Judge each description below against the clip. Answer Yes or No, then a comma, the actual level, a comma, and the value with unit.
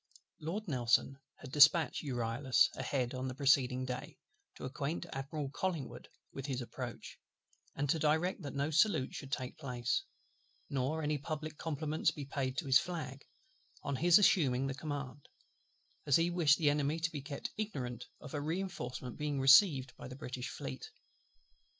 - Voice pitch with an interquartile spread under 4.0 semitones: Yes, average, 3.3 semitones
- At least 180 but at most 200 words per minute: No, average, 160 wpm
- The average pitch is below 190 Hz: Yes, medium, 140 Hz